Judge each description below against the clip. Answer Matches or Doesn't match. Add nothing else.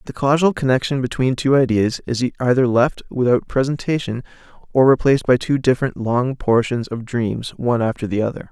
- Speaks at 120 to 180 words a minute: Matches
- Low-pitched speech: Matches